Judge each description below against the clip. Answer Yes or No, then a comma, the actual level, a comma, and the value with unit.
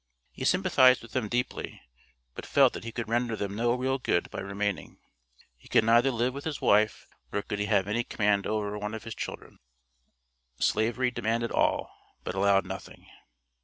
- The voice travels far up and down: No, average, 3.2 semitones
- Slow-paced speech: No, average, 180 wpm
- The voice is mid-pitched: No, low, 115 Hz